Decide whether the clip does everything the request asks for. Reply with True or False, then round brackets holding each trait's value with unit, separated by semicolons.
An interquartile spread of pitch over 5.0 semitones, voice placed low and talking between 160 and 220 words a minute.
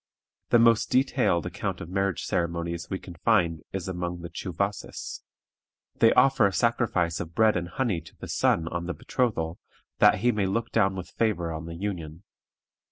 False (4.3 semitones; 90 Hz; 175 wpm)